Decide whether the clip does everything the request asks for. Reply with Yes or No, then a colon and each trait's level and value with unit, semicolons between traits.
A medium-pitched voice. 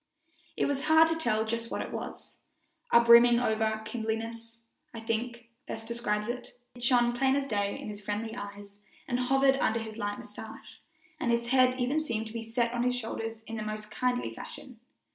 No: high, 235 Hz